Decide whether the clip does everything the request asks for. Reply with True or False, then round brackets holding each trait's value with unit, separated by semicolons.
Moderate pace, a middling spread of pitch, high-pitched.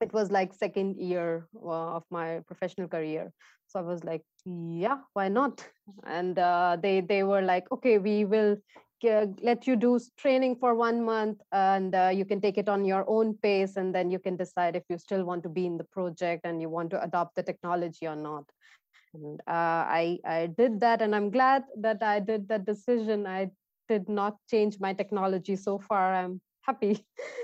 True (195 wpm; 3.5 semitones; 195 Hz)